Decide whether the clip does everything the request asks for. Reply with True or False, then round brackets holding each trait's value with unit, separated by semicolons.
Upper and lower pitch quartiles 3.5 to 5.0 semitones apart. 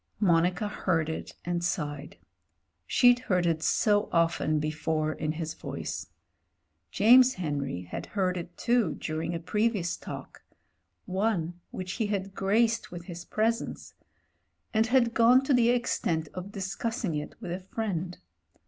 False (5.4 semitones)